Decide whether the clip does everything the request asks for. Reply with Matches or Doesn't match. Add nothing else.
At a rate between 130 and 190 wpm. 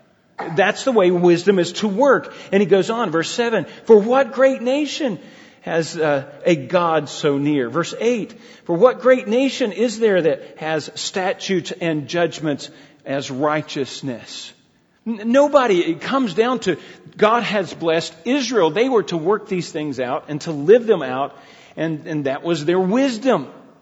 Matches